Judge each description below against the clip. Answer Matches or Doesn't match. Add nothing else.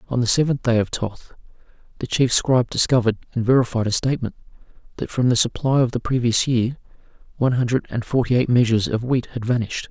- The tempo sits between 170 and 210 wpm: Matches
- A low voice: Matches